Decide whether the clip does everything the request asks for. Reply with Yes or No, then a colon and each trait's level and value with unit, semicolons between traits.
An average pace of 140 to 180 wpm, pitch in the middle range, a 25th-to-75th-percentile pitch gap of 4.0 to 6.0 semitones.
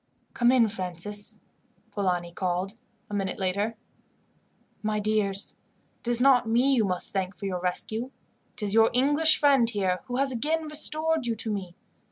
No: average, 165 wpm; high, 215 Hz; average, 4.7 semitones